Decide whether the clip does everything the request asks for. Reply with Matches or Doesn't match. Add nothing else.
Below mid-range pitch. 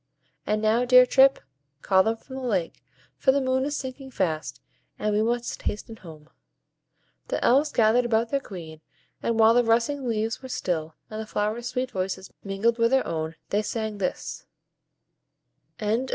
Doesn't match